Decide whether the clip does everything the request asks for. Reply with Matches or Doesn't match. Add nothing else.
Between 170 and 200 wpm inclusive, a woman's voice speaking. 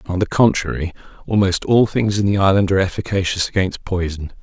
Doesn't match